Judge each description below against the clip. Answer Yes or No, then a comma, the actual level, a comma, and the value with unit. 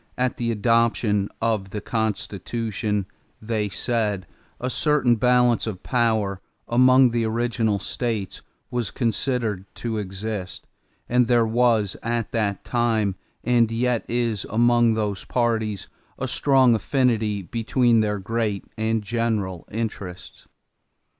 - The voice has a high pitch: No, low, 115 Hz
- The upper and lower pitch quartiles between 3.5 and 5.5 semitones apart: No, narrow, 2.4 semitones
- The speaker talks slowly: Yes, slow, 120 wpm